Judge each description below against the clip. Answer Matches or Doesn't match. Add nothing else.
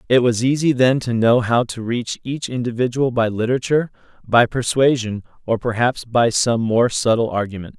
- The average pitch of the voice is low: Matches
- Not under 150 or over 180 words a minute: Matches